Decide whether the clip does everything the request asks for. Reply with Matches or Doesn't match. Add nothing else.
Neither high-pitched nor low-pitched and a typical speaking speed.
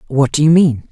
Doesn't match